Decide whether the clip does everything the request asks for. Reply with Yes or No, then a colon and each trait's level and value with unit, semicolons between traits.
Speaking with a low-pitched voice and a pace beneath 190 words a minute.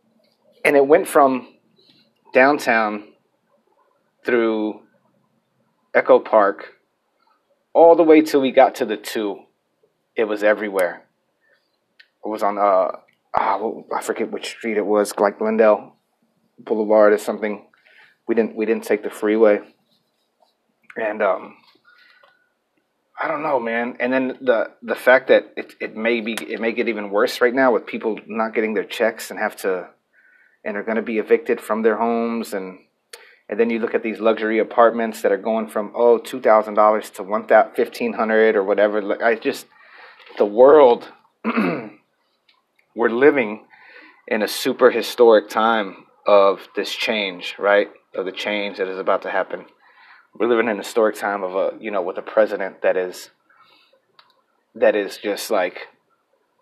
Yes: low, 115 Hz; average, 155 wpm